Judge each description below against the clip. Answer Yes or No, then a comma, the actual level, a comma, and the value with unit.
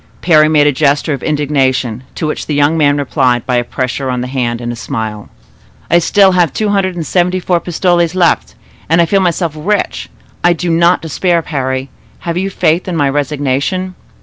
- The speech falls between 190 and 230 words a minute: Yes, average, 200 wpm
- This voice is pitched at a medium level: Yes, medium, 155 Hz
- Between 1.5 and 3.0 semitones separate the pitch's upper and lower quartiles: No, average, 4.6 semitones